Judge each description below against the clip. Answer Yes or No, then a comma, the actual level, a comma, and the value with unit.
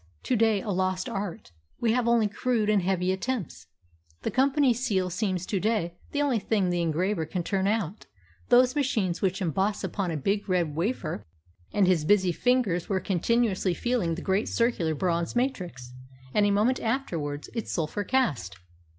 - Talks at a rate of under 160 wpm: No, average, 170 wpm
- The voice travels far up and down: No, average, 4.9 semitones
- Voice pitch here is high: Yes, high, 195 Hz